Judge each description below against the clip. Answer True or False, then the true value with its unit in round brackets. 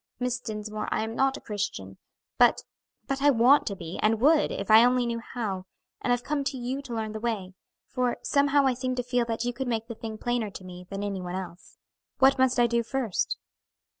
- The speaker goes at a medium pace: False (225 wpm)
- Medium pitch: False (235 Hz)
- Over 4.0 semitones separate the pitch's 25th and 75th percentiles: False (3.2 semitones)